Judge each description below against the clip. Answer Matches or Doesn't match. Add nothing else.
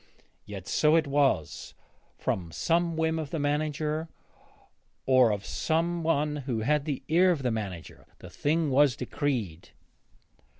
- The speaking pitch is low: Doesn't match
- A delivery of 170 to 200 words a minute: Doesn't match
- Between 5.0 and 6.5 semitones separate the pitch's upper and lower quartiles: Doesn't match